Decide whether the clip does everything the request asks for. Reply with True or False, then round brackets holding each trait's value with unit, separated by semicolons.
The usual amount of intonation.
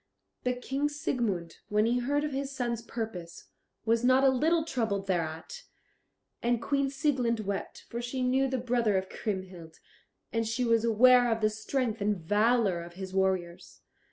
True (4.6 semitones)